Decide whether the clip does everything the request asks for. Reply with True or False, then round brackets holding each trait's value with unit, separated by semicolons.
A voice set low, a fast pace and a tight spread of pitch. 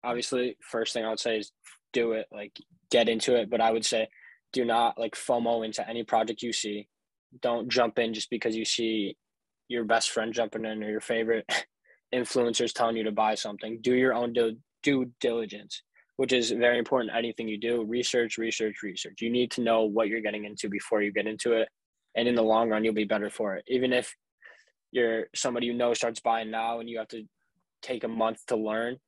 True (115 Hz; 215 wpm; 1.4 semitones)